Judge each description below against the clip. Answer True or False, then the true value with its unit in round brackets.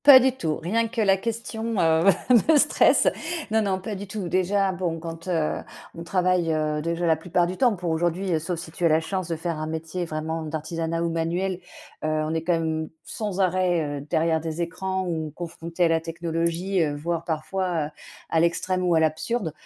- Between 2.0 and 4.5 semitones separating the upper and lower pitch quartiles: True (2.6 semitones)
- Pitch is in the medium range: True (170 Hz)